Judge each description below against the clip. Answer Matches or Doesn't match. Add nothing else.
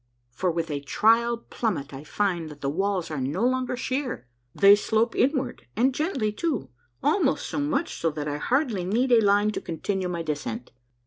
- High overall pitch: Matches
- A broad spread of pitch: Matches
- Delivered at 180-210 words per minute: Matches